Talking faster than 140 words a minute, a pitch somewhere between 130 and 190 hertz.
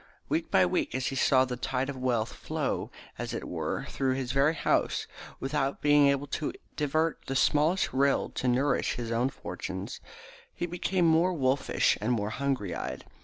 Yes: average, 175 wpm; low, 135 Hz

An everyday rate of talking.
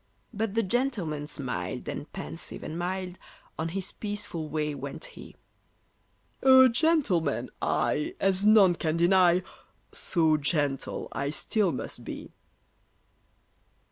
No: slow, 115 wpm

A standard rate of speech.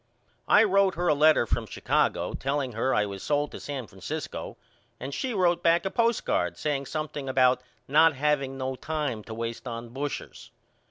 Yes: average, 175 wpm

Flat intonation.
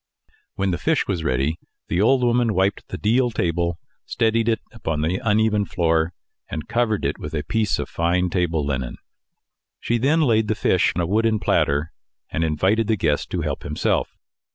No: wide, 5.6 semitones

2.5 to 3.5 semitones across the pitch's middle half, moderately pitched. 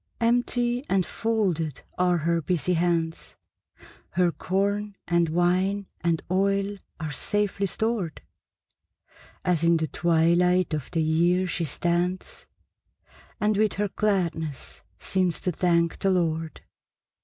Yes: average, 3.0 semitones; medium, 180 Hz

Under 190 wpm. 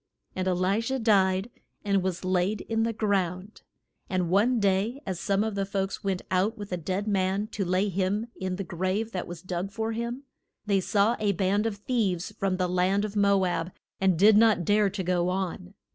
No: fast, 205 wpm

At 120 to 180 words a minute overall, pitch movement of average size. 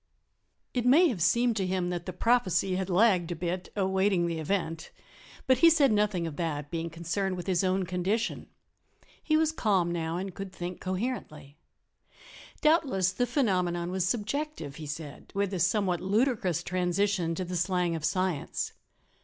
Yes: average, 165 wpm; average, 3.3 semitones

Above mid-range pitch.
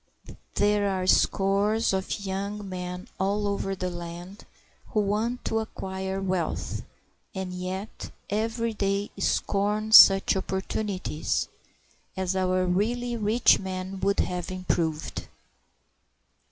Yes: high, 195 Hz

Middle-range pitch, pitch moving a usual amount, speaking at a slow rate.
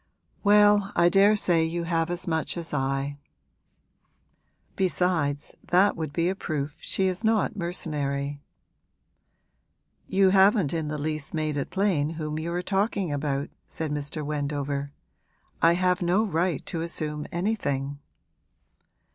Yes: medium, 165 Hz; average, 4.2 semitones; slow, 130 wpm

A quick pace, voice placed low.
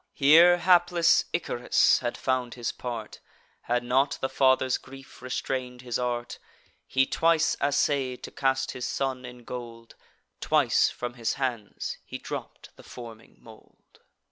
No: average, 140 wpm; low, 125 Hz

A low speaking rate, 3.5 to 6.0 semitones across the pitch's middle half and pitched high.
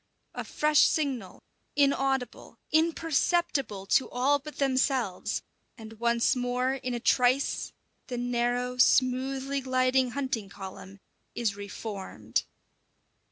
No: slow, 105 wpm; average, 2.7 semitones; very high, 255 Hz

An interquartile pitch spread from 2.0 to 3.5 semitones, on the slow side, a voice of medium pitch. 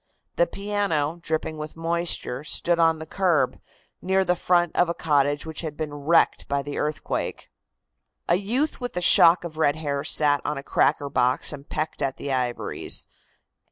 No: average, 3.2 semitones; average, 175 wpm; medium, 155 Hz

